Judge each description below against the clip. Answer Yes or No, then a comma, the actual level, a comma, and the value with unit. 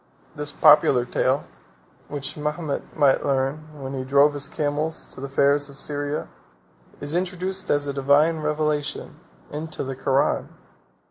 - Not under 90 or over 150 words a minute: Yes, average, 140 wpm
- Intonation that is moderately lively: No, narrow, 1.7 semitones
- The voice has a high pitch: No, medium, 145 Hz